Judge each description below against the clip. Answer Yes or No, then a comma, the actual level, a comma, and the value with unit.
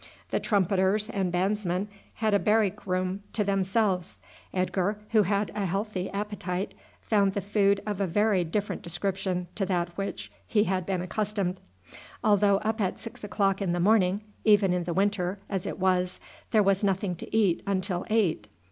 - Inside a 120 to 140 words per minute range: No, average, 175 wpm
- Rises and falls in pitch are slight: Yes, narrow, 2.2 semitones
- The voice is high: Yes, high, 195 Hz